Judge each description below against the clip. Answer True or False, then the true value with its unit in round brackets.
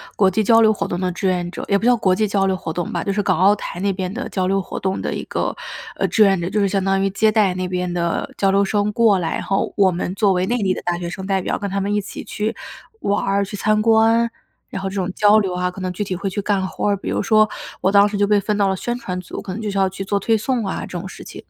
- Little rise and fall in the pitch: True (2.1 semitones)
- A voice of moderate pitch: False (195 Hz)